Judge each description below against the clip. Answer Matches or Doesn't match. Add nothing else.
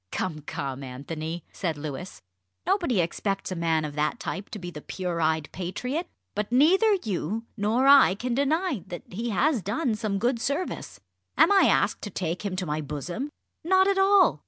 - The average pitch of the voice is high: Matches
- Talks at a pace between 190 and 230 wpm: Doesn't match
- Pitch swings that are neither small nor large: Doesn't match